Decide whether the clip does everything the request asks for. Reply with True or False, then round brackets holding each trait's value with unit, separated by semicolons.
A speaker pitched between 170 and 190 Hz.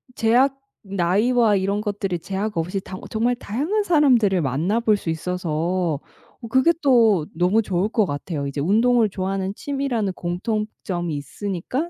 False (200 Hz)